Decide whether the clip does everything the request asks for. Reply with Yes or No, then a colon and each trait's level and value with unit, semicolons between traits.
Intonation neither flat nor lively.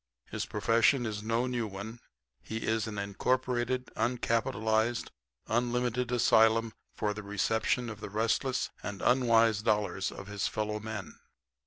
No: narrow, 2.3 semitones